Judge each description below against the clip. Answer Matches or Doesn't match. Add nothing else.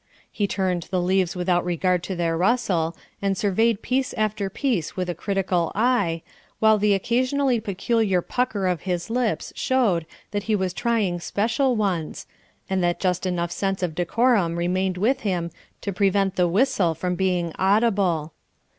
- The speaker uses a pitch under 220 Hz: Matches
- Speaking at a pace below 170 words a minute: Matches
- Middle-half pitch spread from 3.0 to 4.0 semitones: Matches